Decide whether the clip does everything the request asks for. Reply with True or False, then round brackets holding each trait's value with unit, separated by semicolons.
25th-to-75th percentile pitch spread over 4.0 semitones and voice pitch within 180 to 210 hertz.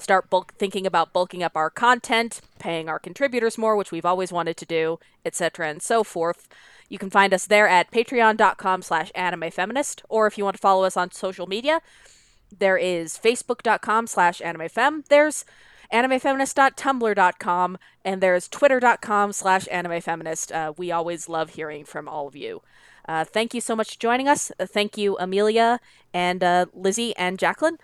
True (4.8 semitones; 190 Hz)